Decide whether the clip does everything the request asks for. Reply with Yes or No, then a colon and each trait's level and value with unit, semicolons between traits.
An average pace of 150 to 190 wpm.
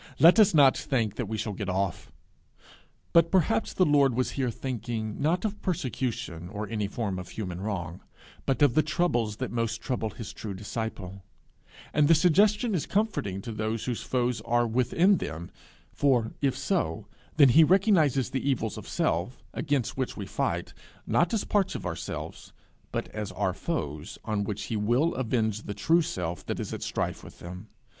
Yes: average, 180 wpm